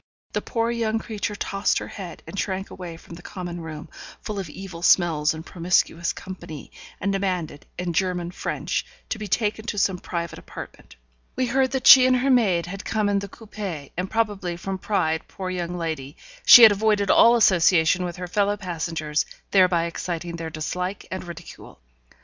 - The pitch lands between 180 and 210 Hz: Yes, medium, 185 Hz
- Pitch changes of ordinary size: Yes, average, 3.3 semitones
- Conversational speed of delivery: Yes, average, 180 wpm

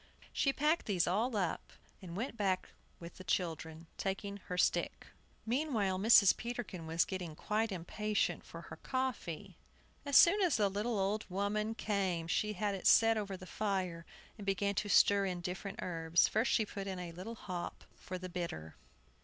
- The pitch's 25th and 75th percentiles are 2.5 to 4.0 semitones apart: Yes, average, 3.2 semitones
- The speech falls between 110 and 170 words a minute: No, average, 180 wpm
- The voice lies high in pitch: Yes, high, 195 Hz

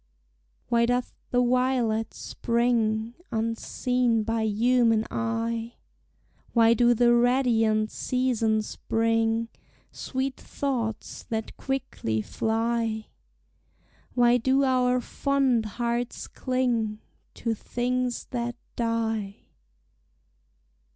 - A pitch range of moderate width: No, narrow, 1.8 semitones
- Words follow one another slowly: Yes, slow, 85 wpm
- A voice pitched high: Yes, high, 235 Hz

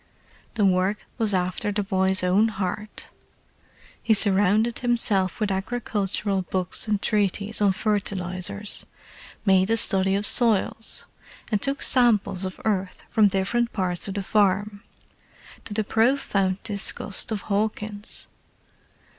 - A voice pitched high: Yes, high, 205 Hz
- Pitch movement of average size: No, narrow, 2.2 semitones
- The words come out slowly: Yes, slow, 120 wpm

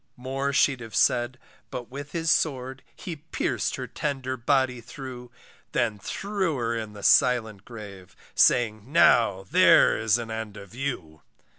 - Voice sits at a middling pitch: No, low, 125 Hz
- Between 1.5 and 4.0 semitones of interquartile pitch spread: Yes, average, 3.7 semitones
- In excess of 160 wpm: No, average, 150 wpm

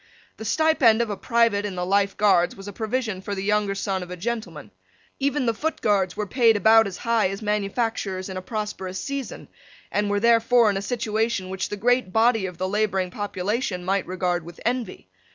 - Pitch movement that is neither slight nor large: Yes, average, 3.3 semitones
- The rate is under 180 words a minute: No, fast, 205 wpm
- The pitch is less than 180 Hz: No, high, 205 Hz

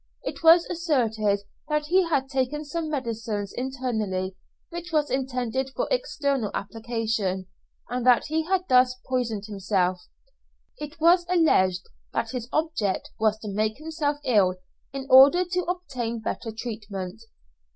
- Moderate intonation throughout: No, wide, 6.1 semitones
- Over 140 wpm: No, slow, 135 wpm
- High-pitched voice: Yes, very high, 255 Hz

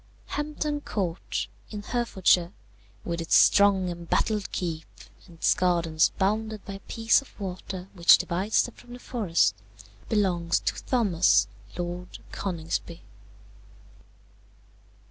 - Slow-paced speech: Yes, slow, 115 wpm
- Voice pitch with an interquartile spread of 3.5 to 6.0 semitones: Yes, average, 3.9 semitones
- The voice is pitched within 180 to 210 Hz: Yes, high, 190 Hz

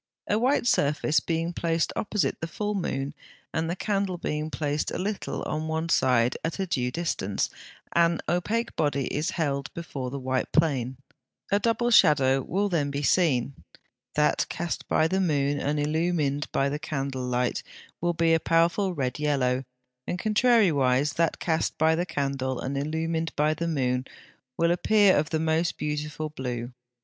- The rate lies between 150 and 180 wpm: Yes, average, 165 wpm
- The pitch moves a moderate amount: Yes, average, 3.6 semitones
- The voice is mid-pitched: Yes, medium, 155 Hz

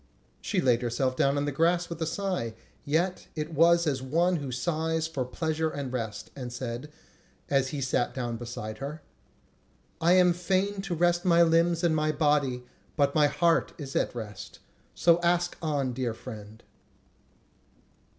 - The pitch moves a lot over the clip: No, average, 4.8 semitones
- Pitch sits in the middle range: Yes, medium, 150 Hz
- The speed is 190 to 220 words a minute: No, average, 170 wpm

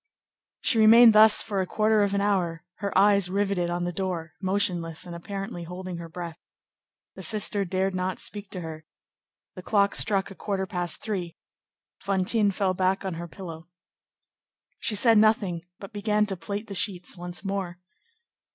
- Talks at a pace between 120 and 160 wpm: No, average, 170 wpm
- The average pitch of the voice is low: No, high, 195 Hz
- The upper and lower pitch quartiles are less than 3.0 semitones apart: Yes, narrow, 2.6 semitones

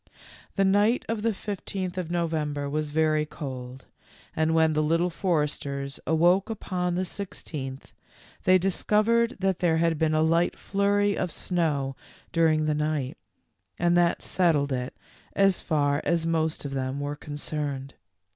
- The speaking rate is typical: Yes, average, 145 wpm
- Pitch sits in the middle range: Yes, medium, 160 Hz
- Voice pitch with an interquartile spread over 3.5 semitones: Yes, average, 3.9 semitones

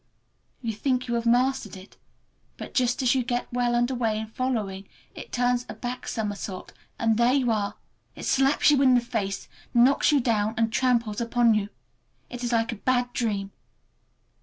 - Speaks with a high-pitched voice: Yes, high, 240 Hz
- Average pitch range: No, narrow, 2.2 semitones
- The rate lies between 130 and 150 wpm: No, average, 185 wpm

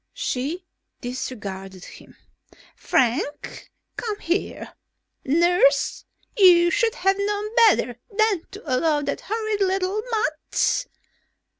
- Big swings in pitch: Yes, wide, 7.1 semitones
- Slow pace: Yes, slow, 100 wpm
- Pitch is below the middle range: No, very high, 360 Hz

